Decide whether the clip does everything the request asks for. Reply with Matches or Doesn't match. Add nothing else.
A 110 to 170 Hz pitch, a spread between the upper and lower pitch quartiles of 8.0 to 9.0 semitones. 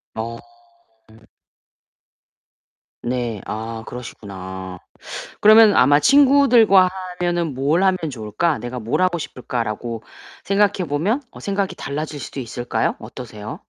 Matches